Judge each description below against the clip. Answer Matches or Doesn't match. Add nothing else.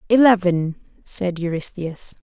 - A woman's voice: Matches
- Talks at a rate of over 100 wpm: Doesn't match